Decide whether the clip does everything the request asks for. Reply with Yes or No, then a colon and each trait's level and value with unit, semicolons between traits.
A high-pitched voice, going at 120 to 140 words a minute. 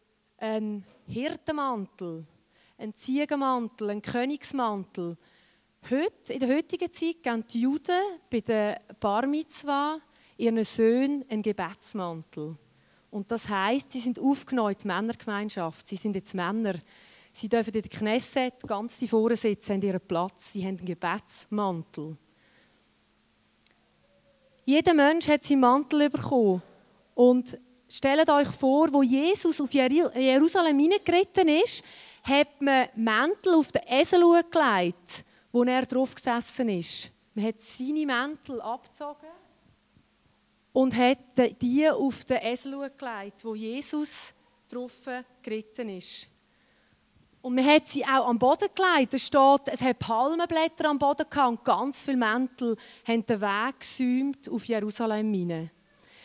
Yes: very high, 250 Hz; slow, 125 wpm